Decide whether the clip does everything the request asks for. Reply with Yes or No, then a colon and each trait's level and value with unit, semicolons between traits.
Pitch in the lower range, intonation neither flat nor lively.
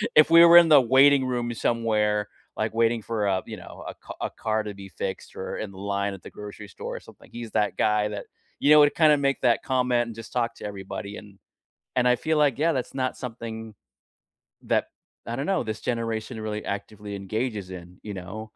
Yes: low, 110 Hz; average, 3.5 semitones